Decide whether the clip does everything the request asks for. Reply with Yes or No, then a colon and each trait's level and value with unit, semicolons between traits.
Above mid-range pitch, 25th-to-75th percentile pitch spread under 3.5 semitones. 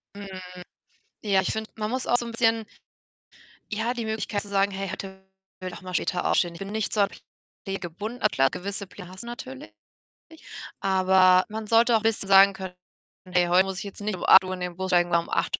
Yes: high, 195 Hz; average, 2.8 semitones